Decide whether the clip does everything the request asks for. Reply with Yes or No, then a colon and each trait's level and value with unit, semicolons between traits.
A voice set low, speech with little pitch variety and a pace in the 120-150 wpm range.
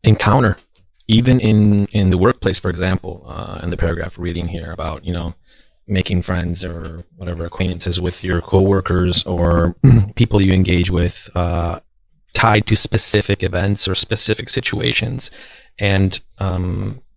No: very low, 95 Hz; average, 3.1 semitones; average, 140 wpm